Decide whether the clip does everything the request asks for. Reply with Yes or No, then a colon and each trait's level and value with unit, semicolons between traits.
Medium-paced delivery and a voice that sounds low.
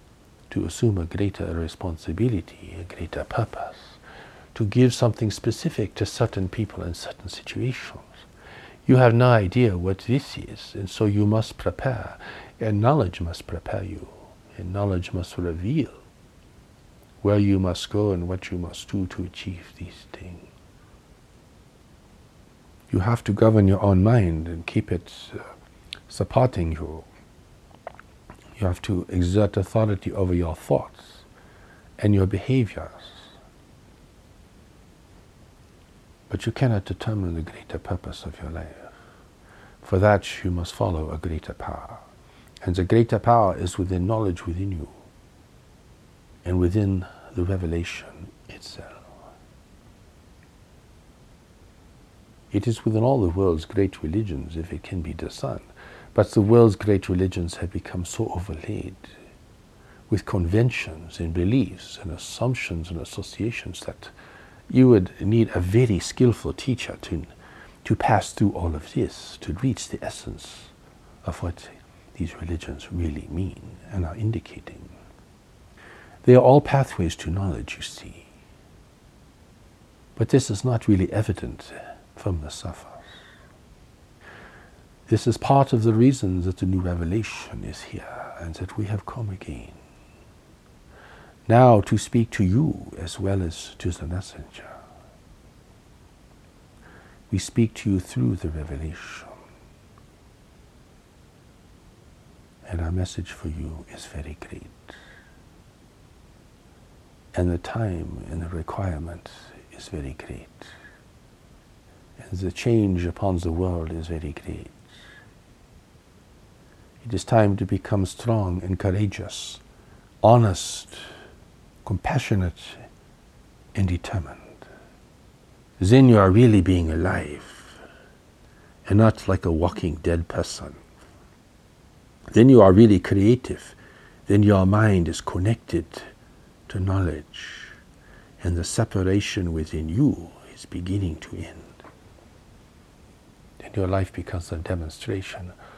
No: slow, 120 wpm; very low, 95 Hz